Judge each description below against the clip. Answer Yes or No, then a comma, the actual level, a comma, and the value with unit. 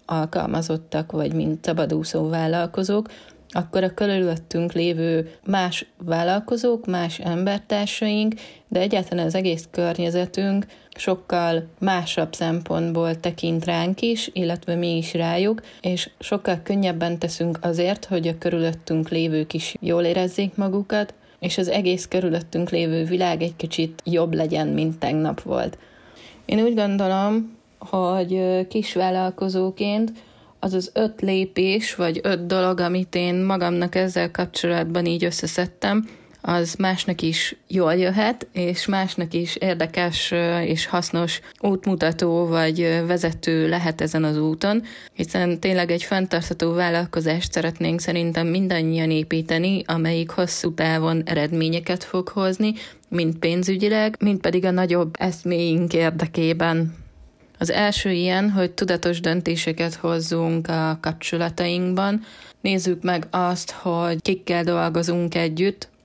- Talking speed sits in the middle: Yes, average, 120 wpm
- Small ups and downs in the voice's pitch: Yes, narrow, 2.1 semitones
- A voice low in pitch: No, medium, 175 Hz